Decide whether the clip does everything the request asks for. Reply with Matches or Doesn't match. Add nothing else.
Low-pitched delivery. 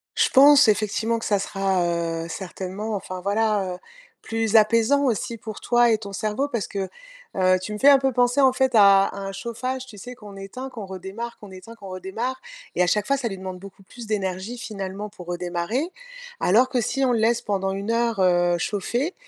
Doesn't match